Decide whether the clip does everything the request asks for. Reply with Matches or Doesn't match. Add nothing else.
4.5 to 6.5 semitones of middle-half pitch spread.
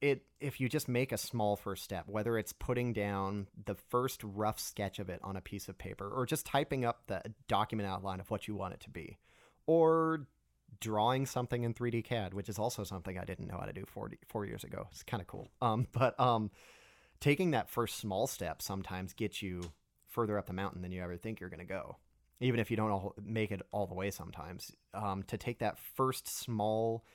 Doesn't match